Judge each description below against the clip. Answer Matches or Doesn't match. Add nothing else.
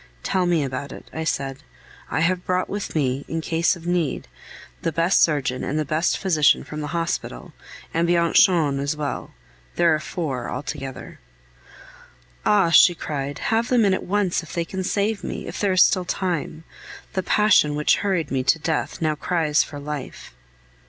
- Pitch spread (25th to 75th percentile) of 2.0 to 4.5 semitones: Matches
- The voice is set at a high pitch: Doesn't match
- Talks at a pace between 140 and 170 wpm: Doesn't match